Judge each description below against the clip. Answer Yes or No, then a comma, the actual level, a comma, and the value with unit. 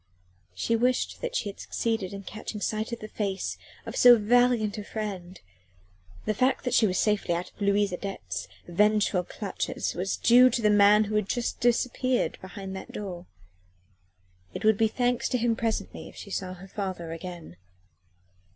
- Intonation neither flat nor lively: Yes, average, 3.3 semitones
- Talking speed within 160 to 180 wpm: Yes, average, 175 wpm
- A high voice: Yes, high, 210 Hz